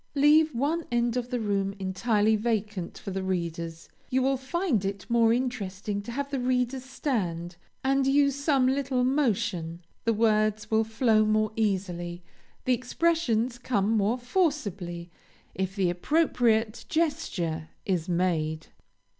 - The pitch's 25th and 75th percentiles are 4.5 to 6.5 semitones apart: Yes, wide, 5.4 semitones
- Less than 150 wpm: Yes, average, 140 wpm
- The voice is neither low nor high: No, high, 220 Hz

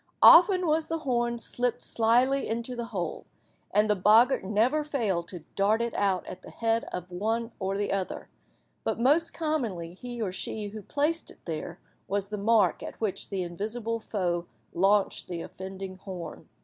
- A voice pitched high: Yes, high, 215 Hz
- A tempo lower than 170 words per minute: No, average, 175 wpm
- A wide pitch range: No, average, 4.1 semitones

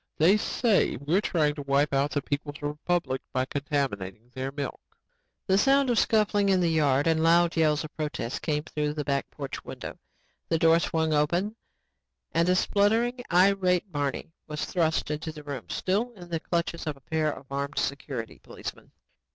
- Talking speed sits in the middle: Yes, average, 180 wpm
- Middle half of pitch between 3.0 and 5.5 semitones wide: Yes, average, 4.0 semitones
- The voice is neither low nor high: Yes, medium, 155 Hz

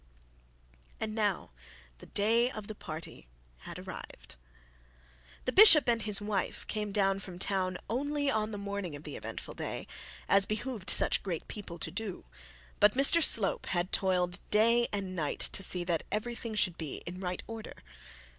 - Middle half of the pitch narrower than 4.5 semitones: Yes, average, 3.4 semitones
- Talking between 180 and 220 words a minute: No, average, 165 wpm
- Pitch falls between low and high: No, high, 205 Hz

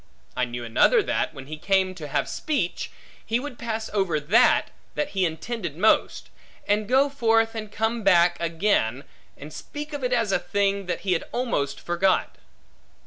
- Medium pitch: No, high, 200 Hz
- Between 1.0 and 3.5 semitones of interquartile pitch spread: No, wide, 5.5 semitones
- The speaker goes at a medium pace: Yes, average, 180 wpm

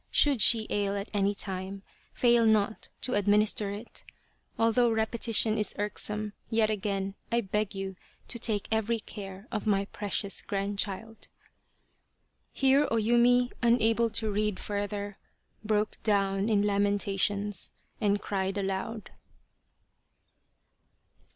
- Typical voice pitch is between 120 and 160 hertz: No, high, 210 Hz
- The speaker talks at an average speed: No, slow, 120 wpm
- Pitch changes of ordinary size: No, narrow, 2.0 semitones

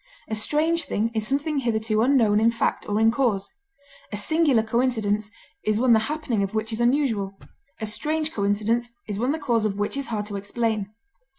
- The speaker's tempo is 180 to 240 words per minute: Yes, average, 190 wpm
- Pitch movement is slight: No, average, 3.7 semitones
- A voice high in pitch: Yes, high, 225 Hz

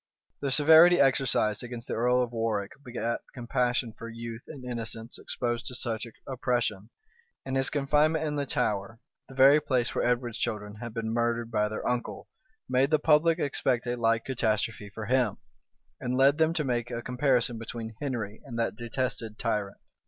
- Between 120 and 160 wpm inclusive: No, average, 175 wpm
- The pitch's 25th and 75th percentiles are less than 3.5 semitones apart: Yes, average, 2.7 semitones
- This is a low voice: Yes, low, 120 Hz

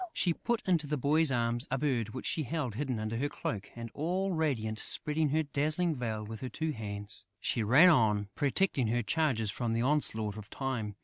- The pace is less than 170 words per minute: No, average, 200 wpm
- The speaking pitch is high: No, low, 130 Hz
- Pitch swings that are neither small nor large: No, wide, 5.7 semitones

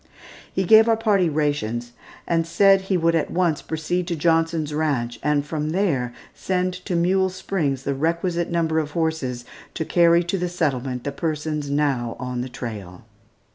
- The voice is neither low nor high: Yes, medium, 160 Hz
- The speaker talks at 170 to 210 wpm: Yes, average, 175 wpm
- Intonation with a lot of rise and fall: No, average, 3.9 semitones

